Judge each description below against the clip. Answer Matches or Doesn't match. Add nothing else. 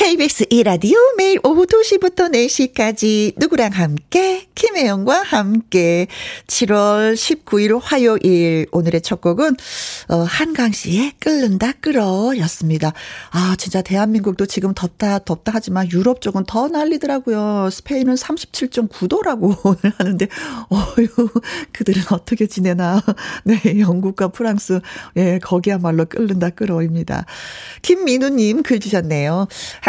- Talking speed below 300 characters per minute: Matches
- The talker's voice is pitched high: Matches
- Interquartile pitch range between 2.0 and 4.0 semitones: Doesn't match